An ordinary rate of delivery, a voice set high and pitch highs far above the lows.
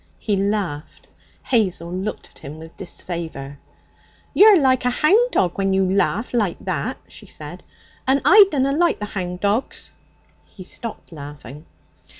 Yes: average, 150 wpm; high, 195 Hz; wide, 7.2 semitones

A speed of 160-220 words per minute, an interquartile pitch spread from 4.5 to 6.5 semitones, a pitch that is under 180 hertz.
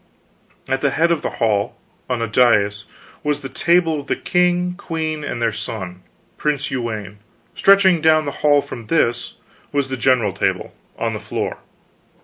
Yes: average, 165 wpm; wide, 5.6 semitones; medium, 140 Hz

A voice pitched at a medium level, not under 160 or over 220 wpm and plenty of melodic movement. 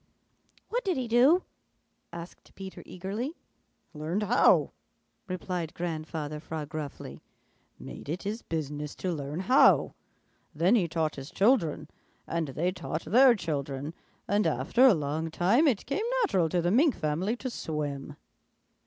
No: medium, 175 Hz; average, 140 wpm; wide, 6.4 semitones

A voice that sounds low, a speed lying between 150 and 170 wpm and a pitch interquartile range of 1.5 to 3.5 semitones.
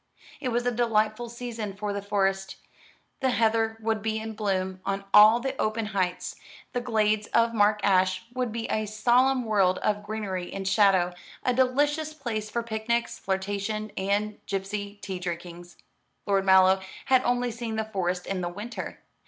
No: high, 215 Hz; average, 165 wpm; average, 3.1 semitones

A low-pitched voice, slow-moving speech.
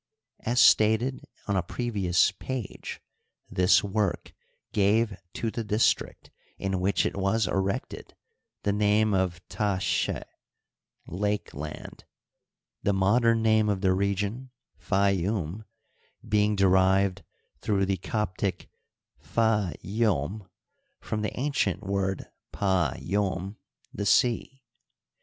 Yes: low, 100 Hz; slow, 110 wpm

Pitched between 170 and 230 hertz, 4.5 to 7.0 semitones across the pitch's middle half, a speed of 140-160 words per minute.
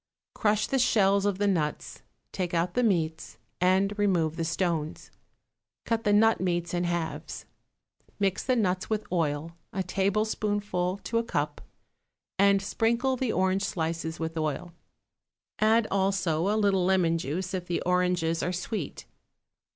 No: medium, 185 Hz; average, 3.5 semitones; average, 145 wpm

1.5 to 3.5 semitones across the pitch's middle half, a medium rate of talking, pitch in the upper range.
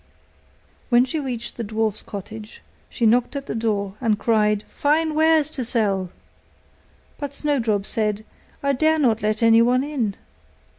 No: average, 4.6 semitones; average, 145 wpm; high, 230 Hz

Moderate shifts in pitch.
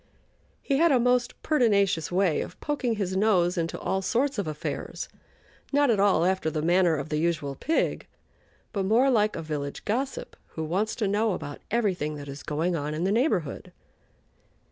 No: wide, 6.4 semitones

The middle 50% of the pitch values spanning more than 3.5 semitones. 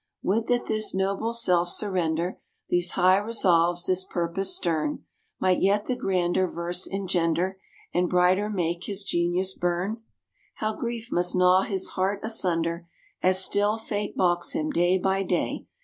No: narrow, 2.6 semitones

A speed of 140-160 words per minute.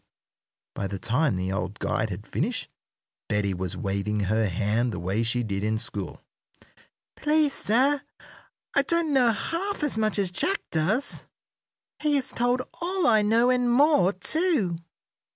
Yes: average, 150 wpm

